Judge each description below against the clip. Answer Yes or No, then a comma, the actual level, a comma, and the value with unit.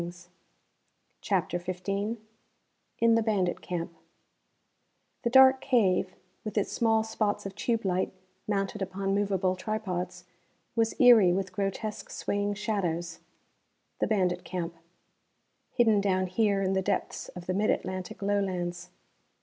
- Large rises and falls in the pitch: No, average, 2.8 semitones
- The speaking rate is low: Yes, slow, 125 wpm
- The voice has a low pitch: No, high, 195 Hz